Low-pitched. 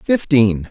Yes: low, 125 Hz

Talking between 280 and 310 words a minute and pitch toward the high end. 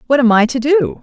Yes: fast, 290 wpm; very high, 255 Hz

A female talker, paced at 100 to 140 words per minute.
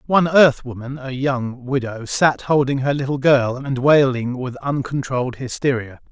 No: male; slow, 135 wpm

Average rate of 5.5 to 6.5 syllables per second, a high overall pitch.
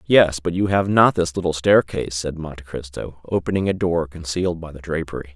No: 5.7 syllables/s; very low, 85 Hz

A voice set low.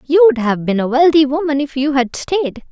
No: very high, 285 Hz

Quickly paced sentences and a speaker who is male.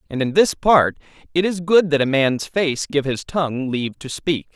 Yes: fast, 225 wpm; male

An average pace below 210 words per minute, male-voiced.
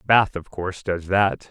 Yes: average, 200 wpm; male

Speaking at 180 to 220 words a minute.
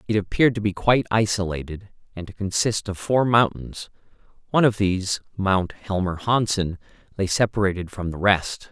No: average, 160 wpm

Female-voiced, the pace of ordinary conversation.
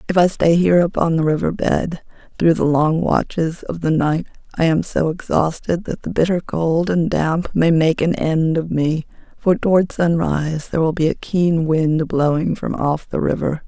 Yes: female; average, 195 wpm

